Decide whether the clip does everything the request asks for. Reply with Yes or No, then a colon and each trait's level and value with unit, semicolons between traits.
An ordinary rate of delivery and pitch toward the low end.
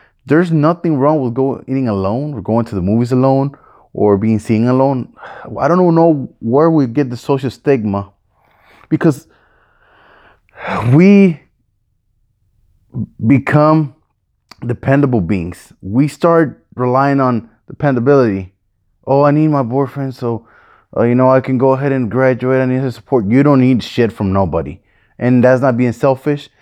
Yes: average, 150 wpm; low, 130 Hz